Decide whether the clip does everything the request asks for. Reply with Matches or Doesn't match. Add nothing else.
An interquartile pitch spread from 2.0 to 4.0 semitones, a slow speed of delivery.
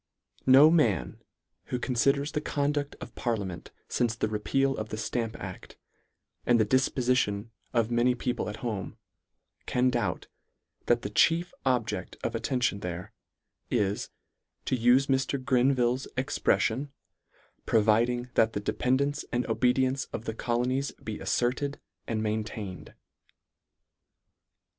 Matches